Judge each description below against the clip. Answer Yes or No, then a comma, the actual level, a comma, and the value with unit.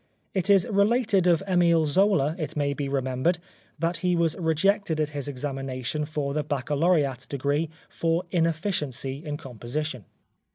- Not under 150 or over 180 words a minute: No, average, 140 wpm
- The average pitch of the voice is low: No, medium, 155 Hz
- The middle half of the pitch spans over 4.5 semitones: No, average, 3.8 semitones